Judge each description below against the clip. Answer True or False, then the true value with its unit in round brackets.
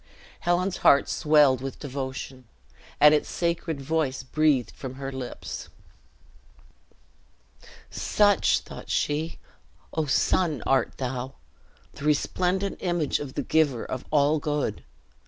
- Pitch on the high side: False (145 Hz)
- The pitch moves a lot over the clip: False (3.2 semitones)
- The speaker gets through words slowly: True (115 wpm)